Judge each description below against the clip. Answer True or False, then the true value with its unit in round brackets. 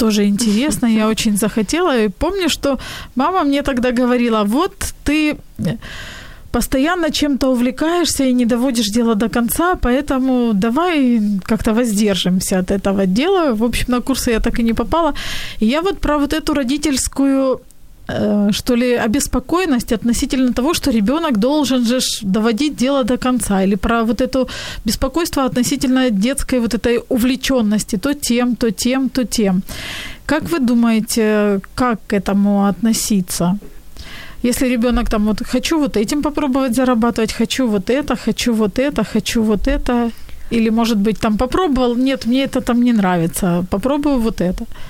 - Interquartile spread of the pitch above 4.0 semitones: False (3.4 semitones)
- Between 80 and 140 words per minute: False (150 wpm)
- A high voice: True (245 Hz)